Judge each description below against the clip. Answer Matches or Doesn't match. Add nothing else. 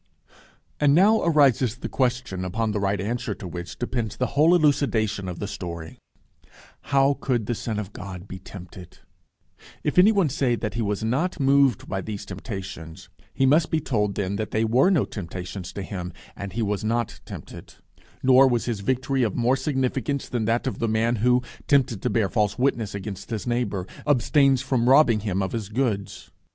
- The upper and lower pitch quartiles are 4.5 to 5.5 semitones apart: Matches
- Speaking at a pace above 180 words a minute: Matches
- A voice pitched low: Matches